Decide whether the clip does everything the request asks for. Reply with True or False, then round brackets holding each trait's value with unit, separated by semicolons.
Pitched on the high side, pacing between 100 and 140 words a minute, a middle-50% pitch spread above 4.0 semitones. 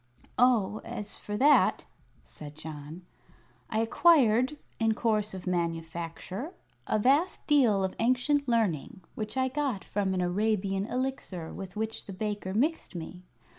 True (210 Hz; 135 wpm; 5.3 semitones)